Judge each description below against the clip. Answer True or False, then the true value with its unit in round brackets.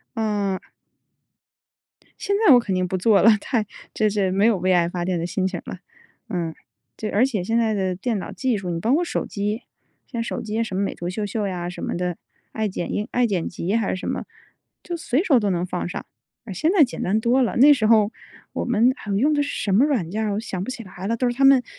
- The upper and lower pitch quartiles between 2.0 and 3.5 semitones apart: False (4.3 semitones)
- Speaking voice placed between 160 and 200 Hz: False (210 Hz)